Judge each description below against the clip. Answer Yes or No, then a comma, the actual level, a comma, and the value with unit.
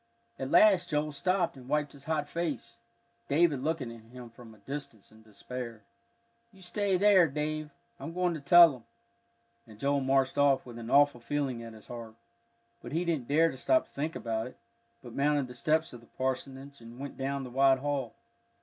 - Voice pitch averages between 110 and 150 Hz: Yes, medium, 140 Hz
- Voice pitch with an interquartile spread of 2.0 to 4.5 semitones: Yes, average, 3.9 semitones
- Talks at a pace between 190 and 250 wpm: Yes, average, 195 wpm